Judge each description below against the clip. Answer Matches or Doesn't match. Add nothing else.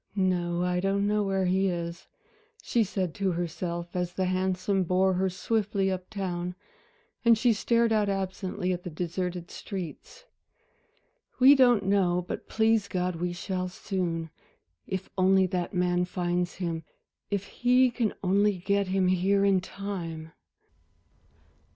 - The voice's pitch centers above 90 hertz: Matches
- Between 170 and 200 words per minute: Doesn't match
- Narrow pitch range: Matches